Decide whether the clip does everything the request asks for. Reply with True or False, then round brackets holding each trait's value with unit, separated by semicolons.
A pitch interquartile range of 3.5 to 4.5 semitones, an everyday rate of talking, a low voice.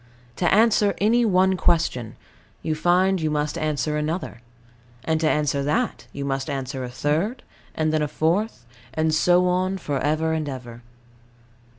False (4.0 semitones; 160 wpm; 155 Hz)